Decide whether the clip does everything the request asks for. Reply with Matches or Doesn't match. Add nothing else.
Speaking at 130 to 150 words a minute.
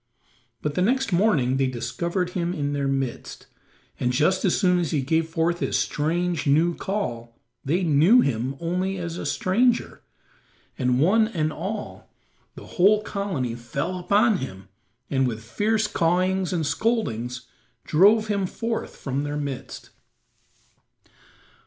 Matches